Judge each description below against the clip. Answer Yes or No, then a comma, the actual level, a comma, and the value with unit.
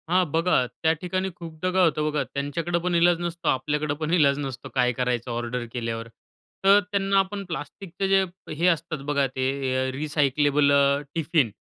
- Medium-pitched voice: Yes, medium, 150 Hz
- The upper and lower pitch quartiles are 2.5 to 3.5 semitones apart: No, average, 4.1 semitones